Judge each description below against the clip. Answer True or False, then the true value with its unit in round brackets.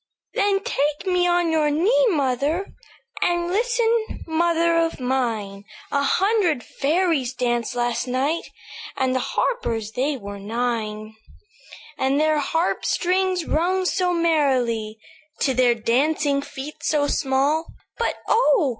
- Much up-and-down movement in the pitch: True (5.9 semitones)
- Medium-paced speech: False (125 wpm)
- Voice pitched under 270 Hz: False (295 Hz)